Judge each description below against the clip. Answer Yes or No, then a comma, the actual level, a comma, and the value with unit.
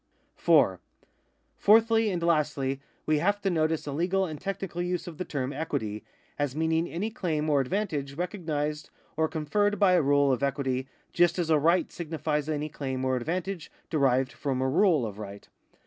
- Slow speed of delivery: No, average, 180 wpm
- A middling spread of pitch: Yes, average, 4.2 semitones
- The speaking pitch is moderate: Yes, medium, 155 Hz